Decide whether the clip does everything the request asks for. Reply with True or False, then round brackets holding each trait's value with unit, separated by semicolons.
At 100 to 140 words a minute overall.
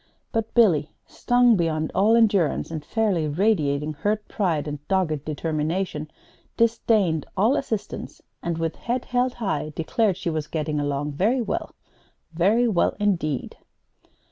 True (135 wpm)